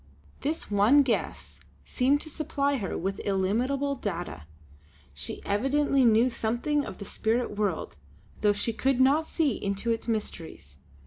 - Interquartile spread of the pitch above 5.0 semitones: Yes, wide, 5.5 semitones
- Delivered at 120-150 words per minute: Yes, average, 140 wpm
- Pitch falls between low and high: No, high, 230 Hz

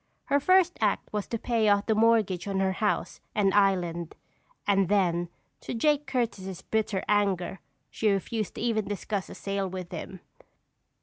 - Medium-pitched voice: No, high, 205 Hz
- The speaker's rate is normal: Yes, average, 165 wpm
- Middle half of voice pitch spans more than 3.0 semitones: No, average, 2.7 semitones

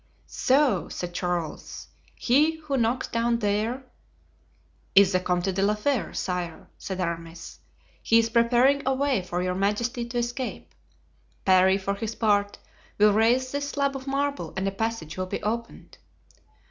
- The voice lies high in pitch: Yes, high, 225 Hz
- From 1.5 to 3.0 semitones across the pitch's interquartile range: No, average, 5.2 semitones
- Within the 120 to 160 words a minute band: Yes, average, 155 wpm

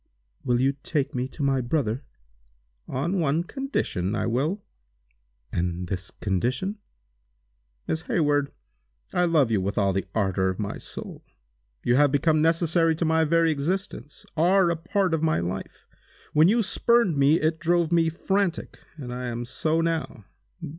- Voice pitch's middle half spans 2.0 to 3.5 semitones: No, wide, 5.6 semitones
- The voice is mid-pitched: Yes, medium, 155 Hz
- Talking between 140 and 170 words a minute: Yes, average, 155 wpm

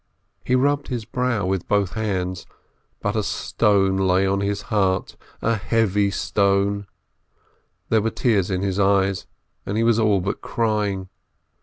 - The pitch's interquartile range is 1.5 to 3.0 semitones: Yes, narrow, 2.4 semitones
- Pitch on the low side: Yes, low, 100 Hz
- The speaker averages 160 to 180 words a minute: No, average, 150 wpm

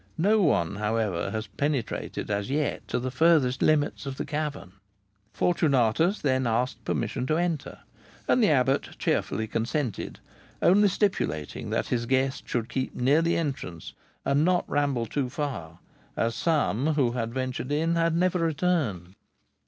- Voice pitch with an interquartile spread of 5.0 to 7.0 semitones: Yes, wide, 5.4 semitones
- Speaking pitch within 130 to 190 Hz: Yes, low, 135 Hz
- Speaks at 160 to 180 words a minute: No, average, 150 wpm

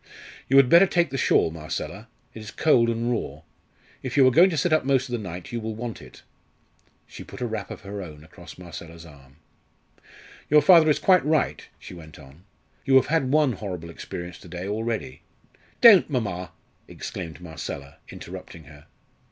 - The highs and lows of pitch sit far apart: Yes, wide, 7.9 semitones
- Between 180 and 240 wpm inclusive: Yes, average, 190 wpm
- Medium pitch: No, low, 110 Hz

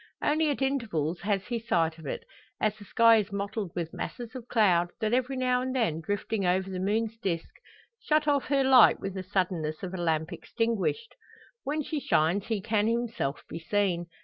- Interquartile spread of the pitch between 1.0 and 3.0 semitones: No, average, 5.2 semitones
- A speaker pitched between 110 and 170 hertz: No, high, 210 Hz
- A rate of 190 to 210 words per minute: Yes, average, 195 wpm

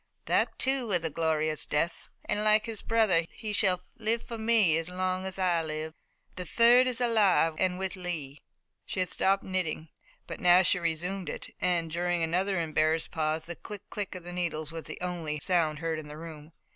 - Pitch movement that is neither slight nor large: Yes, average, 3.3 semitones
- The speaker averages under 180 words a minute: No, average, 195 wpm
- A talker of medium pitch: Yes, medium, 180 Hz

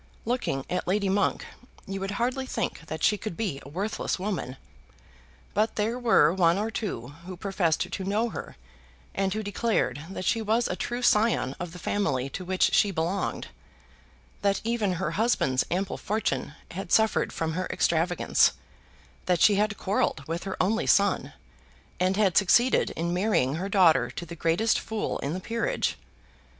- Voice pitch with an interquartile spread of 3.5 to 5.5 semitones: Yes, average, 4.2 semitones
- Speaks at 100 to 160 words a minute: No, average, 170 wpm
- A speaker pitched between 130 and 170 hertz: No, high, 195 Hz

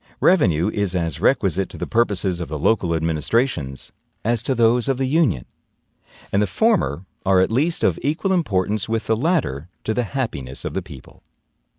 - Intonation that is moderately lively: No, wide, 7.2 semitones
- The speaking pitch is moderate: No, low, 105 Hz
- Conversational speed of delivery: Yes, average, 180 wpm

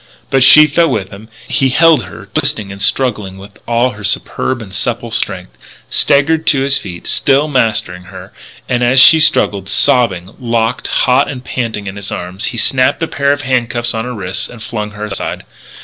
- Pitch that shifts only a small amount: No, average, 4.7 semitones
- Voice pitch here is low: Yes, low, 120 Hz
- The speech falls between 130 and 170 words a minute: No, average, 190 wpm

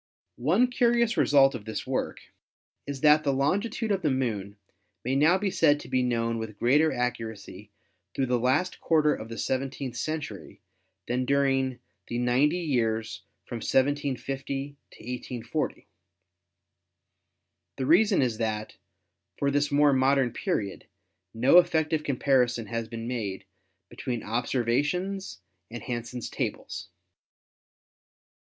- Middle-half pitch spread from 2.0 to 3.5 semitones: No, average, 3.9 semitones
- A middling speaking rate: No, slow, 130 wpm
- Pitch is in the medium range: No, low, 130 Hz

